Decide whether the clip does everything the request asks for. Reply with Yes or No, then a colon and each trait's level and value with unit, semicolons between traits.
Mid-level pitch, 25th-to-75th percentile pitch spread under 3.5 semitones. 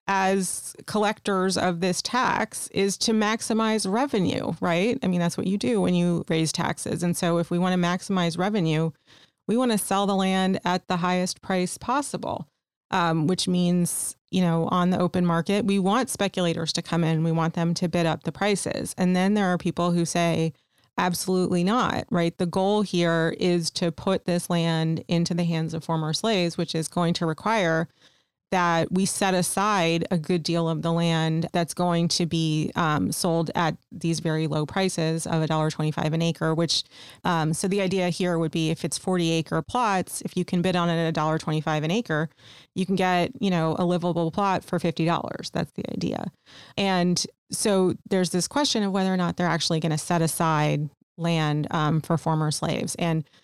Yes: medium, 175 Hz; narrow, 2.4 semitones